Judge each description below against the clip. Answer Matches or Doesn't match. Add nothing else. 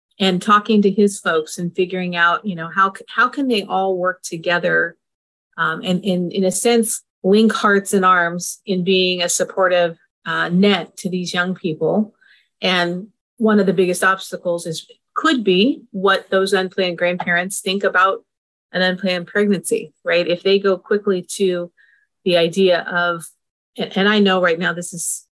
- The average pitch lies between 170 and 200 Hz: Matches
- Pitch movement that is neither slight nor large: Doesn't match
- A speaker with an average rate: Matches